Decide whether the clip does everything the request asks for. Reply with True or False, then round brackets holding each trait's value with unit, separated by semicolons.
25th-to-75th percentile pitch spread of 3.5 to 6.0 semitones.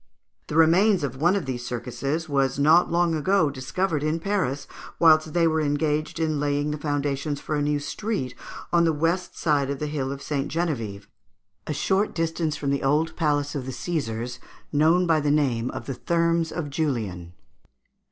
False (3.0 semitones)